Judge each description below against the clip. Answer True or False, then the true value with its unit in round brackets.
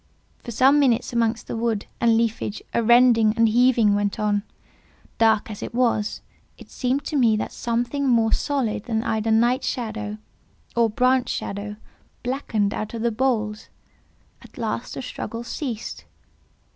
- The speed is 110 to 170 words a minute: True (155 wpm)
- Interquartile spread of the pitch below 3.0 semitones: True (2.5 semitones)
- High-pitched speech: True (230 Hz)